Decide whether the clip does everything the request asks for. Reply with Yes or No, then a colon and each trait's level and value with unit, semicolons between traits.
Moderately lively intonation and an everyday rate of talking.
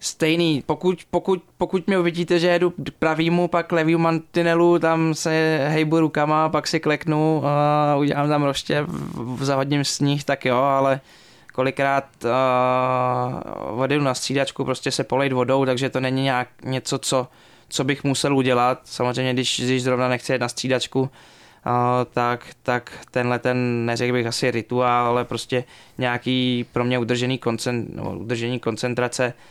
Yes: average, 3.6 semitones; average, 155 wpm